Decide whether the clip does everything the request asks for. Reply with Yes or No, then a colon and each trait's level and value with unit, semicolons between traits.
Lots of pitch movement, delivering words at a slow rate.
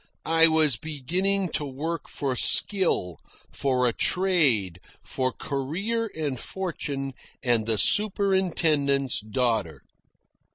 Yes: wide, 5.8 semitones; slow, 100 wpm